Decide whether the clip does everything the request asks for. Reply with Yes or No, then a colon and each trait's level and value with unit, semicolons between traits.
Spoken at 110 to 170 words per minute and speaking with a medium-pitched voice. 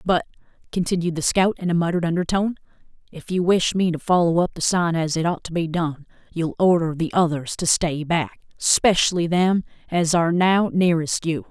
No: average, 190 wpm; medium, 170 Hz